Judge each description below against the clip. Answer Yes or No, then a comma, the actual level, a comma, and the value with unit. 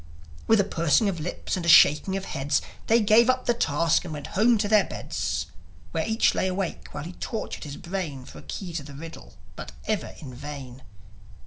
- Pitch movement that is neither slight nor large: No, wide, 6.0 semitones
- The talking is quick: Yes, fast, 210 wpm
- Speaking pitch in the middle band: Yes, medium, 175 Hz